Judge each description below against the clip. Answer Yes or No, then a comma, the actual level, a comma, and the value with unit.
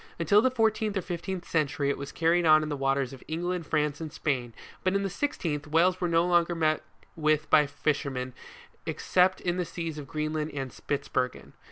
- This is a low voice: No, medium, 155 Hz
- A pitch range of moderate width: Yes, average, 3.4 semitones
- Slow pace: No, average, 195 wpm